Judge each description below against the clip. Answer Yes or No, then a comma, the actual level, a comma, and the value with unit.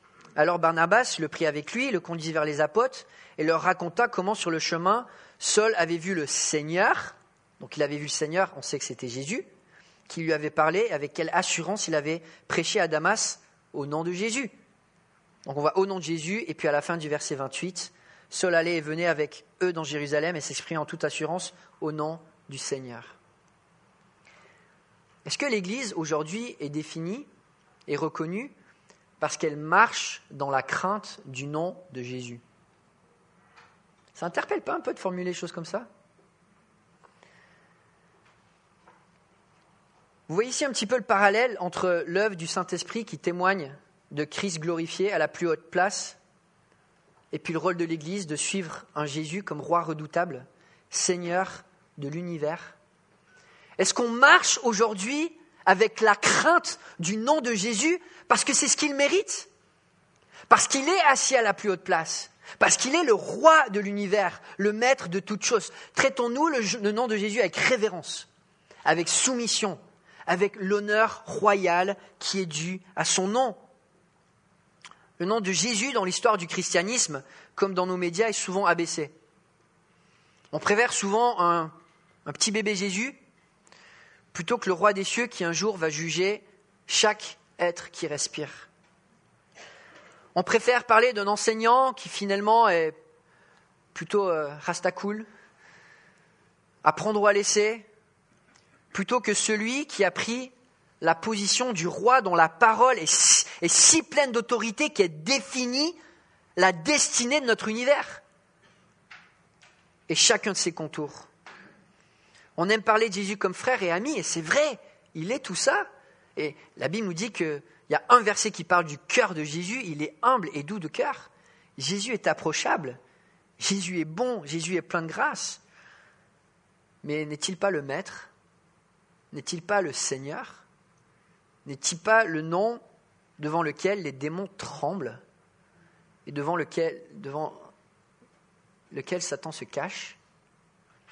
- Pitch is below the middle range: No, medium, 185 Hz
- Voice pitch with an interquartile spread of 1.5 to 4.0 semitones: No, average, 5.2 semitones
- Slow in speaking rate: No, average, 155 wpm